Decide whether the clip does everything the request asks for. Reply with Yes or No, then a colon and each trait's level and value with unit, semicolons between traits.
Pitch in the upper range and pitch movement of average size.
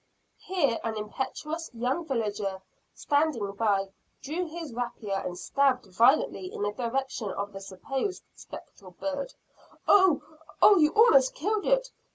No: very high, 265 Hz; wide, 7.4 semitones